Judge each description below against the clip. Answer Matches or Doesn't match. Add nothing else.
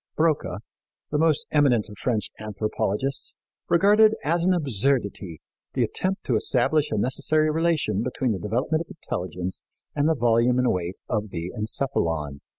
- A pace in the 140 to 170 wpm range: Matches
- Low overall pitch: Matches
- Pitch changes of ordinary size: Doesn't match